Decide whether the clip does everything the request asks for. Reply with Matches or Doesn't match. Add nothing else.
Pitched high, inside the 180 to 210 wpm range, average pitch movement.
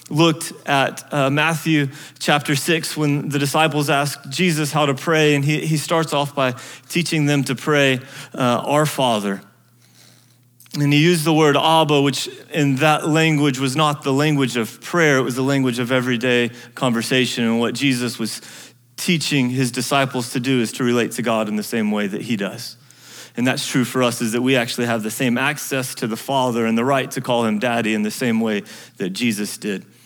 Doesn't match